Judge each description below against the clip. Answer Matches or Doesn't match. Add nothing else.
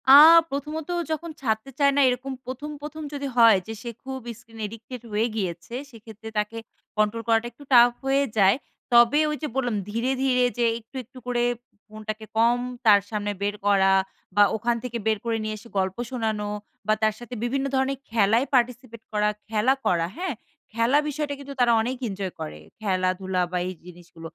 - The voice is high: Matches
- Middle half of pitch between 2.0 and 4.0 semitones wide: Matches